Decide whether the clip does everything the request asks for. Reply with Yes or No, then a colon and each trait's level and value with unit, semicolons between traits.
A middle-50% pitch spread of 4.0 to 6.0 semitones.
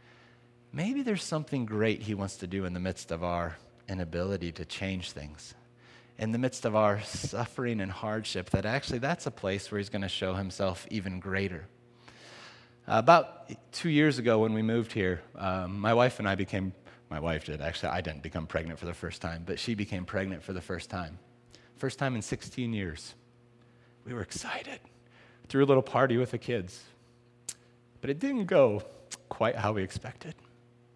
Yes: average, 4.4 semitones